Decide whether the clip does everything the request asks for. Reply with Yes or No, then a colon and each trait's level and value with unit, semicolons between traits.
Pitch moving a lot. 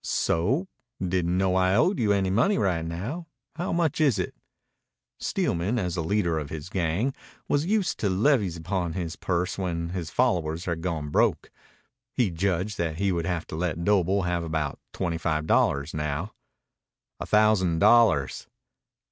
No: average, 4.0 semitones